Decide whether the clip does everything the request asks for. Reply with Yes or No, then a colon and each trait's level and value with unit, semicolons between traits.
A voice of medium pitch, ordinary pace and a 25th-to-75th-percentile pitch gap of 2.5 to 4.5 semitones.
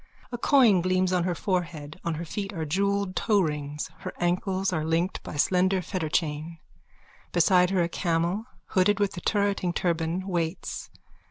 Yes: medium, 180 Hz; average, 160 wpm; average, 2.8 semitones